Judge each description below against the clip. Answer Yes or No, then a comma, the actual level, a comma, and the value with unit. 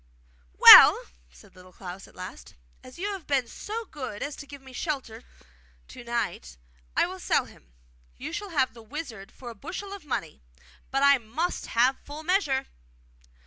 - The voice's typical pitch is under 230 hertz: No, very high, 265 Hz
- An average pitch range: No, wide, 5.8 semitones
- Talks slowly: No, average, 175 wpm